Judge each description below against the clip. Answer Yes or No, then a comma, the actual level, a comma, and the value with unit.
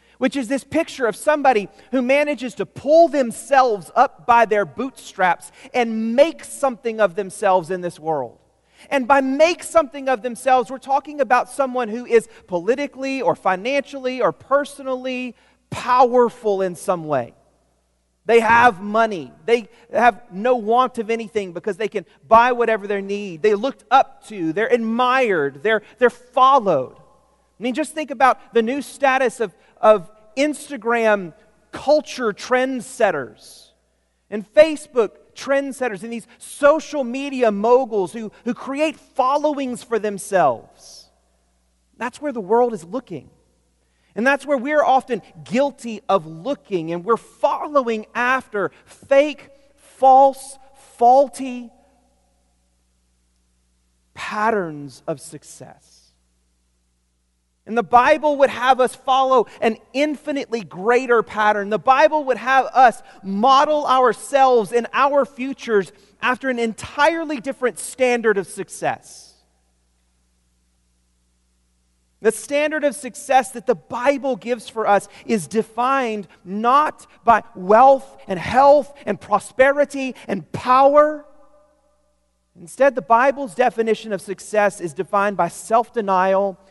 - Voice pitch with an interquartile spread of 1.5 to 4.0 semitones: No, average, 5.3 semitones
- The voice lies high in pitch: Yes, high, 235 Hz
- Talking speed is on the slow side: Yes, slow, 125 wpm